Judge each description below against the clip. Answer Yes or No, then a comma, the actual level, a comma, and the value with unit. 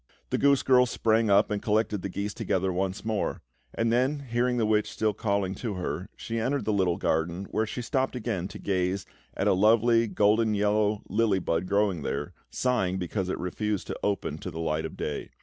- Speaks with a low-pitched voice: Yes, low, 105 Hz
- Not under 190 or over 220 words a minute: Yes, average, 200 wpm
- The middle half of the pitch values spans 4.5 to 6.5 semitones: No, average, 3.4 semitones